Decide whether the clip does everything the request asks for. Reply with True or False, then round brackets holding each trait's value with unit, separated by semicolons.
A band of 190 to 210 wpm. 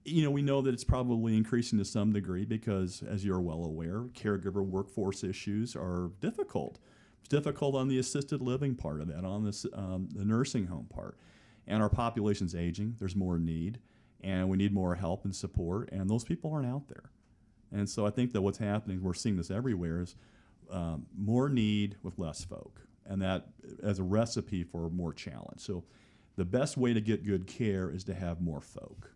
True (200 wpm)